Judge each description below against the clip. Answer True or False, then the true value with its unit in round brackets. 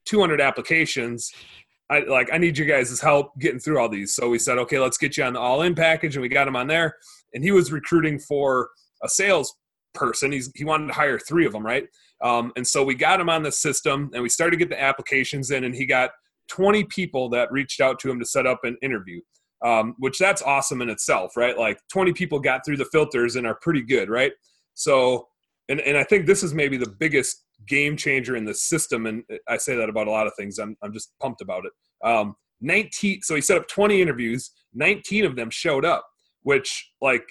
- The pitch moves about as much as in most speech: True (4.7 semitones)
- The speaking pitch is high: False (140 Hz)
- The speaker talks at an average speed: False (230 wpm)